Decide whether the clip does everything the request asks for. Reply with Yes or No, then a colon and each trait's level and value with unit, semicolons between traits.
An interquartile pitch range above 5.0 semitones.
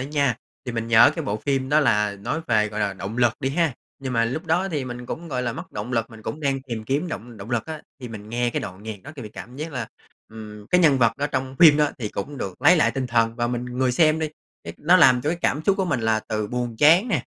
No: average, 4.7 semitones